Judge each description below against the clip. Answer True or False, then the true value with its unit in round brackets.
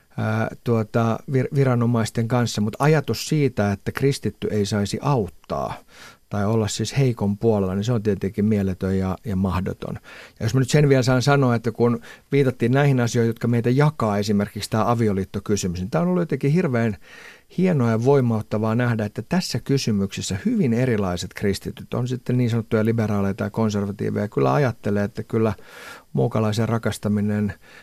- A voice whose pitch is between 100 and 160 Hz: True (115 Hz)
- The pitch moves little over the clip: False (3.4 semitones)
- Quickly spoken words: True (160 wpm)